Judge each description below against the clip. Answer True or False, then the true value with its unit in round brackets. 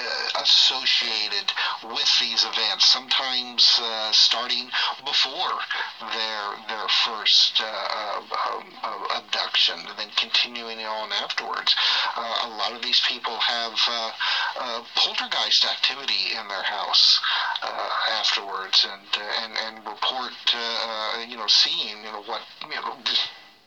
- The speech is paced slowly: True (125 wpm)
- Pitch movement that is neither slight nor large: False (1.3 semitones)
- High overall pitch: False (115 Hz)